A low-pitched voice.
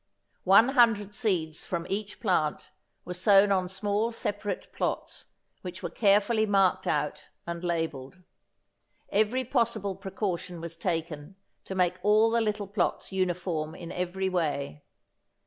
No: high, 190 Hz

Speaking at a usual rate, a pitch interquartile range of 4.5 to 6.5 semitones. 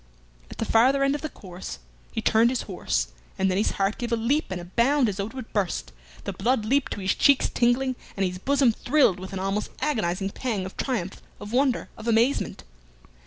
No: fast, 215 wpm; average, 5.2 semitones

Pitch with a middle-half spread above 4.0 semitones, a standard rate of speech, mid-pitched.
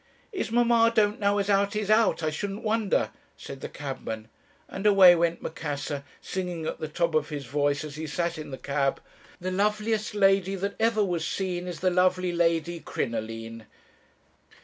Yes: average, 5.2 semitones; average, 175 wpm; medium, 175 Hz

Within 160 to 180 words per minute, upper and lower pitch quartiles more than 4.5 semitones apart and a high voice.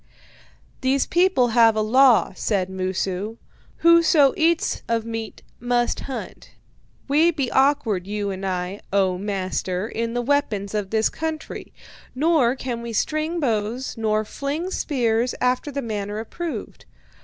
No: slow, 135 wpm; average, 5.1 semitones; high, 230 Hz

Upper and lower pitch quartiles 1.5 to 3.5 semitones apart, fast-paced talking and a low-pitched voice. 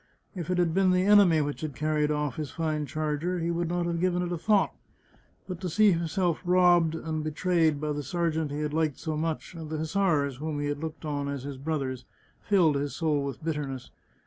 No: average, 2.9 semitones; fast, 225 wpm; medium, 160 Hz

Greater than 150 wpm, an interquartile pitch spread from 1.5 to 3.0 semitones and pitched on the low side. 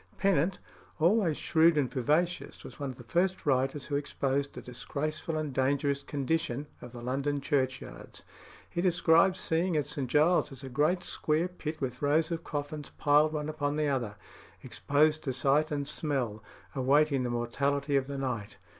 No: average, 165 wpm; average, 2.7 semitones; medium, 145 Hz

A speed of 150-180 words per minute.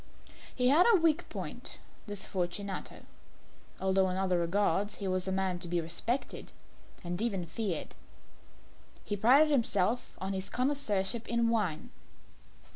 No: slow, 135 wpm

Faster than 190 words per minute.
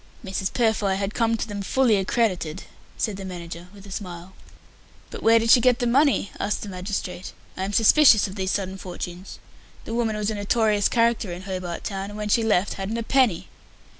Yes: average, 200 wpm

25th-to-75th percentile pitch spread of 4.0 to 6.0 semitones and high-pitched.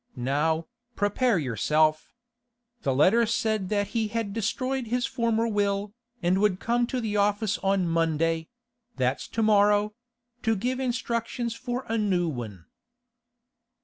Yes: average, 5.1 semitones; high, 210 Hz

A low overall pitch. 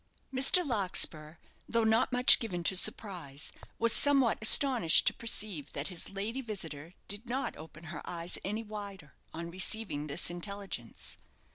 No: high, 195 Hz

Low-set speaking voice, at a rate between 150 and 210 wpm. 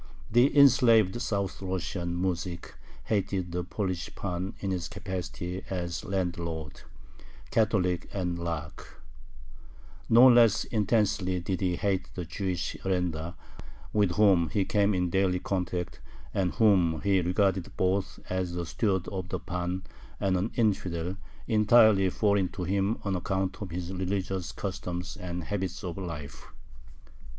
No: very low, 95 Hz; slow, 135 wpm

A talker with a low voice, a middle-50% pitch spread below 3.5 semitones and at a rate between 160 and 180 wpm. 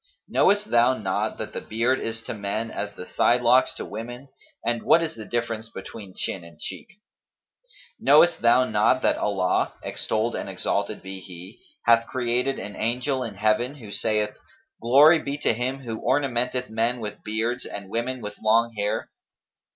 Yes: low, 115 Hz; average, 3.0 semitones; average, 165 wpm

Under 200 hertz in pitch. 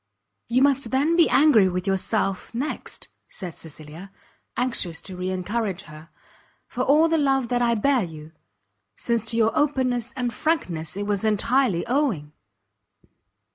No: high, 230 Hz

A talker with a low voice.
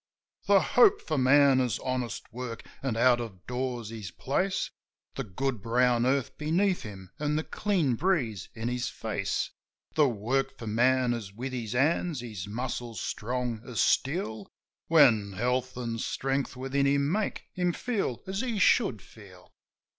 Yes: low, 125 Hz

